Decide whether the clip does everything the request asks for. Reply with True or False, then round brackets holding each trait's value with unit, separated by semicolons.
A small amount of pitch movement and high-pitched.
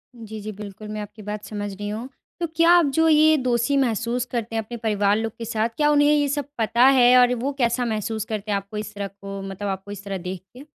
False (3.3 semitones; 220 Hz)